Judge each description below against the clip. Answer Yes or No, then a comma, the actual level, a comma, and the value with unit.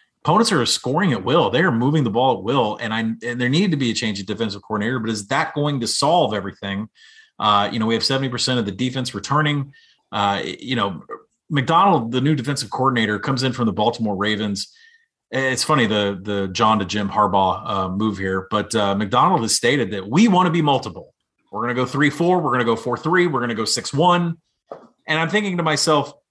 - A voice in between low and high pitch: No, low, 120 Hz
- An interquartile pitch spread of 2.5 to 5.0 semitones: No, wide, 5.6 semitones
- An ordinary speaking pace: No, fast, 230 wpm